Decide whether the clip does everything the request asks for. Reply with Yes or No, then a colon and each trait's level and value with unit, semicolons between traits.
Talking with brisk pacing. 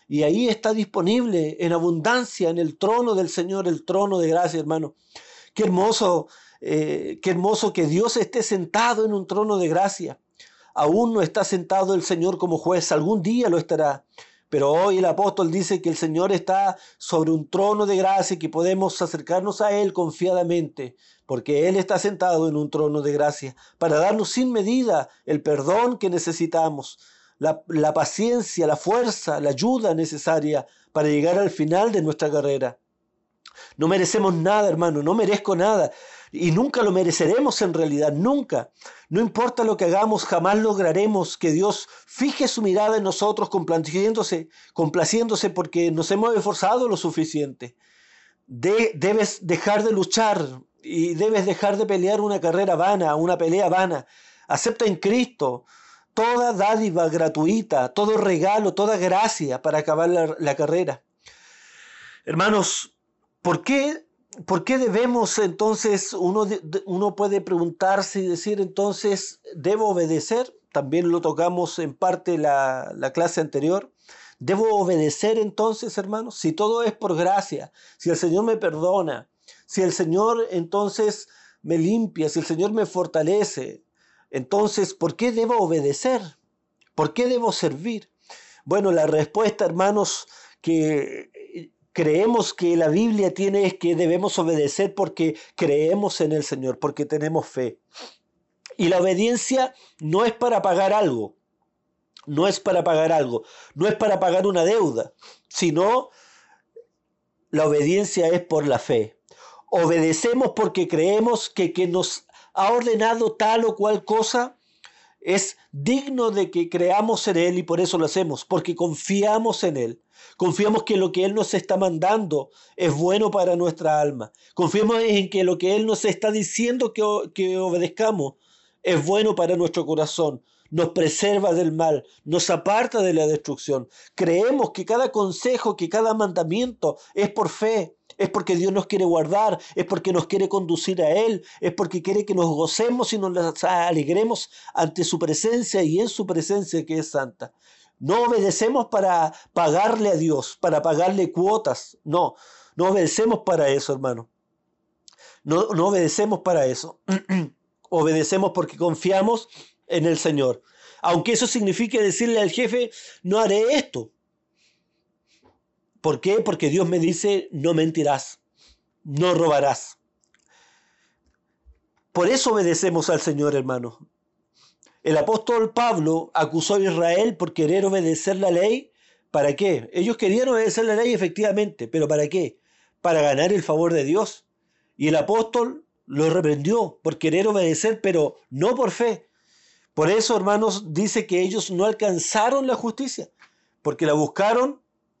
No: average, 150 wpm